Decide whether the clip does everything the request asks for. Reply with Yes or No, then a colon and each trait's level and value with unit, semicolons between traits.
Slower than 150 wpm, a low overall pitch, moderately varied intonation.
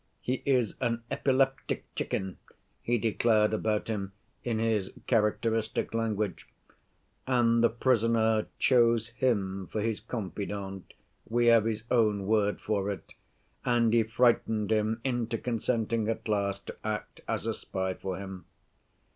No: slow, 135 wpm; low, 110 Hz; narrow, 2.2 semitones